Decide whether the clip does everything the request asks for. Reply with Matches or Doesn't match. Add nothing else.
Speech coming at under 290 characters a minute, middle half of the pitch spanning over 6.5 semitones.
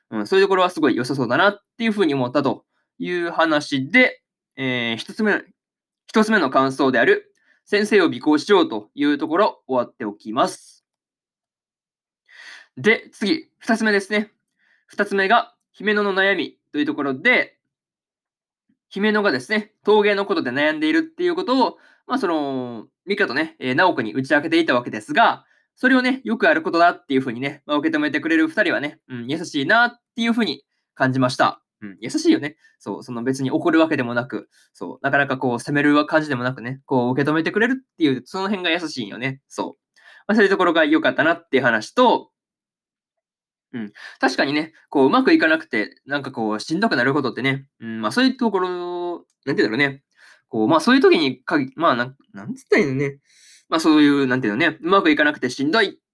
Doesn't match